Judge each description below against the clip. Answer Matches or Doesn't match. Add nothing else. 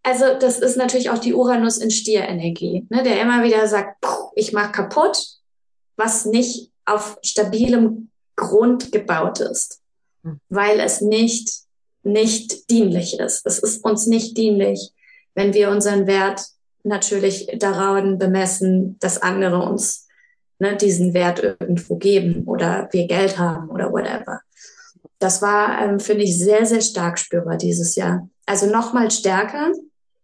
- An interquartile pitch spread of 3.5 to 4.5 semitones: Doesn't match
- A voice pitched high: Matches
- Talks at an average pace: Matches